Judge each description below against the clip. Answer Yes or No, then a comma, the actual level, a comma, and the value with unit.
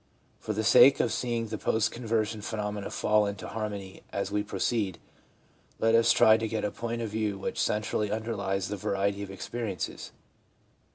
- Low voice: Yes, low, 105 Hz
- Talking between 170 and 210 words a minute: Yes, average, 175 wpm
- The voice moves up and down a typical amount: No, narrow, 1.9 semitones